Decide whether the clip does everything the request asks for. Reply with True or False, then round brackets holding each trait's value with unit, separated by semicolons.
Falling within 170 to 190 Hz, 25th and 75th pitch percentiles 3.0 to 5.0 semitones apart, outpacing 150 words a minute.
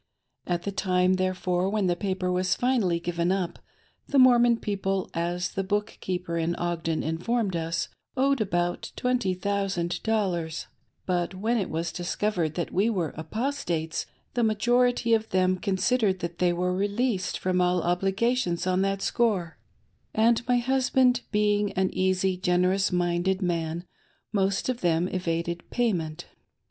False (185 Hz; 3.5 semitones; 145 wpm)